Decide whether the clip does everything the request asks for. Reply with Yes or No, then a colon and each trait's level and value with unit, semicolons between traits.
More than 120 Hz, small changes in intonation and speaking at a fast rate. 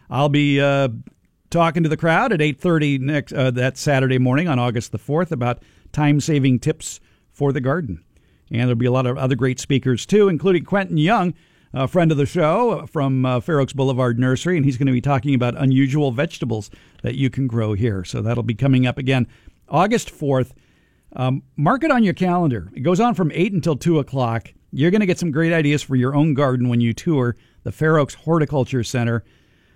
No: low, 135 Hz; average, 4.3 semitones; fast, 210 wpm